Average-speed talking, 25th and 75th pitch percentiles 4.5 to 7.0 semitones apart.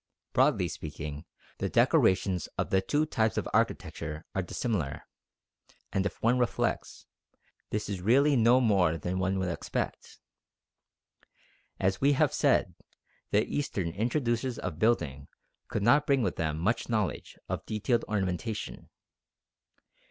No: slow, 130 wpm; average, 5.0 semitones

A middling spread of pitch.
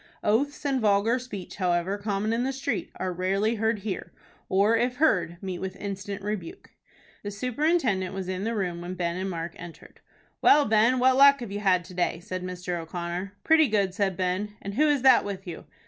Yes: average, 4.4 semitones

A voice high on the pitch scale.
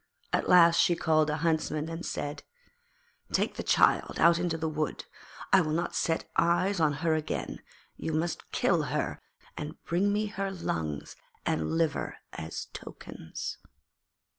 No: medium, 165 Hz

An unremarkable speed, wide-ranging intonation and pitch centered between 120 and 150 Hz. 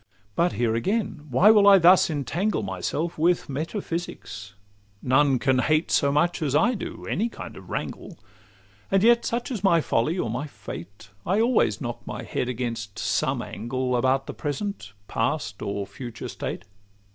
Yes: average, 165 wpm; wide, 7.6 semitones; medium, 140 Hz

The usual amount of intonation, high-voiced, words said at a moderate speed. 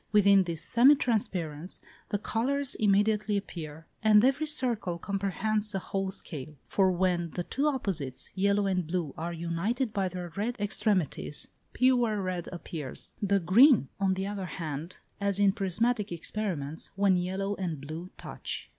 Yes: average, 3.7 semitones; high, 195 Hz; average, 150 wpm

